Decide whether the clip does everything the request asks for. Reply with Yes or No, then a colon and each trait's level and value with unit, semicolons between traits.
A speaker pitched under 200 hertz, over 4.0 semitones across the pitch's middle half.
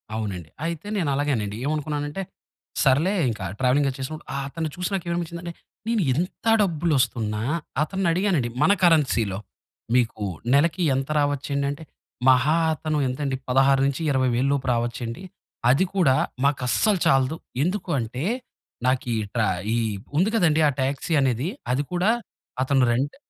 Yes: medium, 140 Hz; average, 4.5 semitones